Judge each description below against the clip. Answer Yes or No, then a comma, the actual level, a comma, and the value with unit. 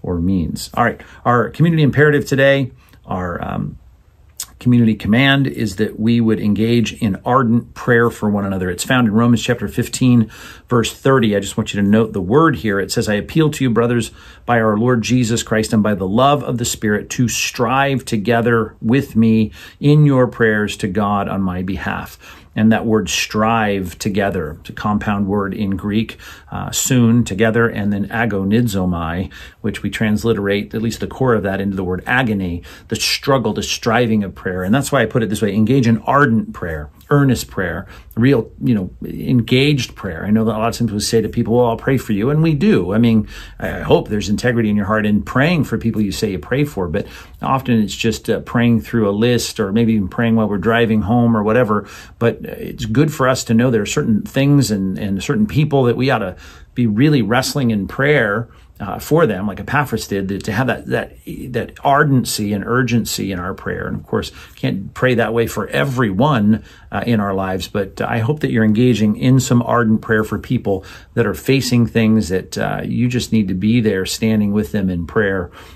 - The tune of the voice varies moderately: Yes, average, 3.1 semitones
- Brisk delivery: Yes, fast, 210 wpm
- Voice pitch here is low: Yes, low, 110 Hz